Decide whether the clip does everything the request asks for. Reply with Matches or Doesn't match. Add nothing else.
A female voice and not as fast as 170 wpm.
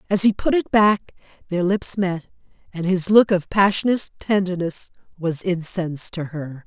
Matches